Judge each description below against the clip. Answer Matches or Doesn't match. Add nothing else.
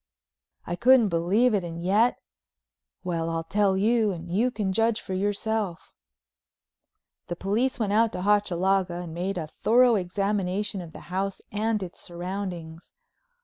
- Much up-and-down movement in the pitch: Doesn't match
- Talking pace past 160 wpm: Doesn't match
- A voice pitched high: Matches